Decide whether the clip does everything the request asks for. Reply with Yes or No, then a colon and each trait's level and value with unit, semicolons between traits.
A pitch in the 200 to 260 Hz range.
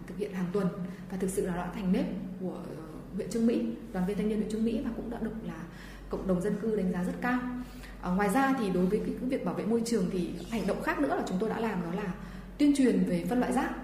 Yes: high, 205 Hz